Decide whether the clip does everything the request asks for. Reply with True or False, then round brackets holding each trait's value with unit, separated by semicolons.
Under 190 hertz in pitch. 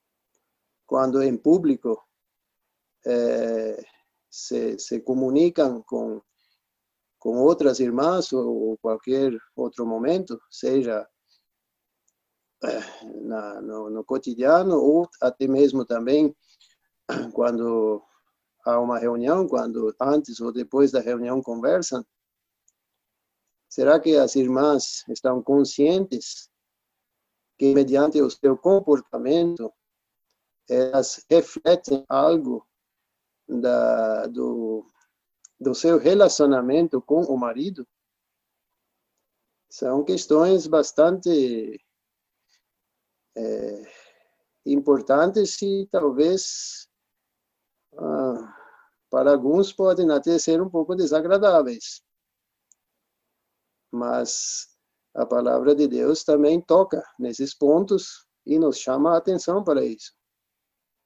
True (140 Hz)